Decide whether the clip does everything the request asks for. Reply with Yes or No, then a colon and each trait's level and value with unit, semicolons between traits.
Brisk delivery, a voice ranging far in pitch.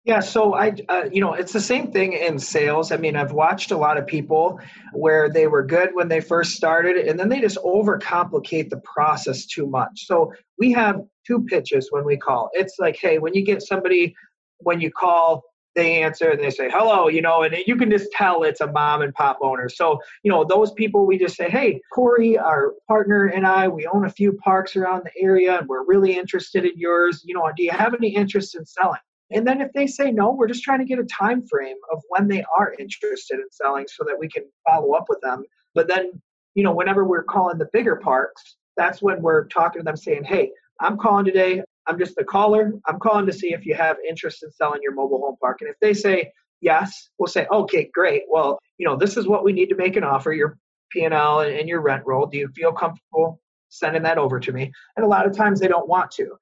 Yes: fast, 240 wpm; wide, 5.7 semitones